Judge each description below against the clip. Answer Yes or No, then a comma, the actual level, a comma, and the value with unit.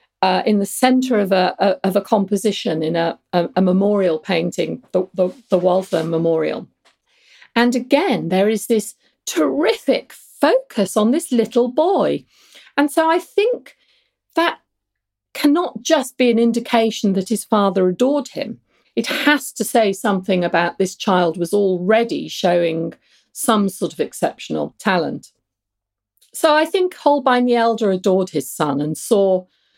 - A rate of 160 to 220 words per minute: No, average, 145 wpm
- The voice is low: No, high, 205 Hz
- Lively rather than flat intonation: Yes, wide, 5.8 semitones